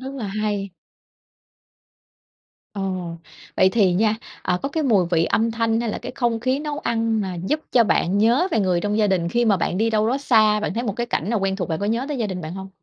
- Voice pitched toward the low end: No, high, 215 Hz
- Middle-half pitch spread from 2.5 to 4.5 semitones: Yes, average, 3.5 semitones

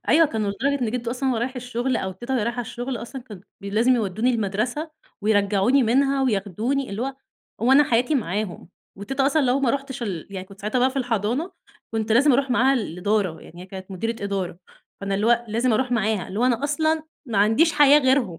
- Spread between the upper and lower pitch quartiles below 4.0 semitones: No, average, 4.6 semitones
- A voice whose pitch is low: No, high, 235 Hz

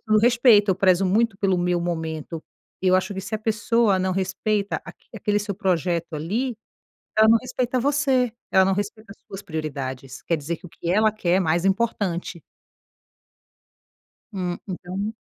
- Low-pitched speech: No, high, 195 Hz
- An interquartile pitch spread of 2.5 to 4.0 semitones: Yes, average, 3.7 semitones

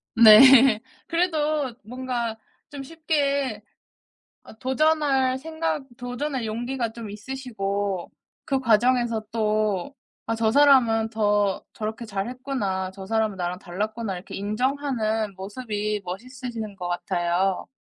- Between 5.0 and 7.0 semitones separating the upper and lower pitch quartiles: No, average, 4.2 semitones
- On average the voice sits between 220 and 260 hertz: Yes, high, 225 Hz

